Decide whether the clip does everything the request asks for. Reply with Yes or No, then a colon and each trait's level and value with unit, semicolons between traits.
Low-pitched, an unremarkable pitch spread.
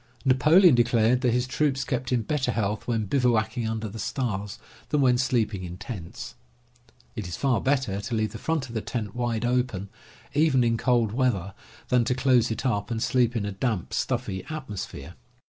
Yes: low, 120 Hz; average, 3.1 semitones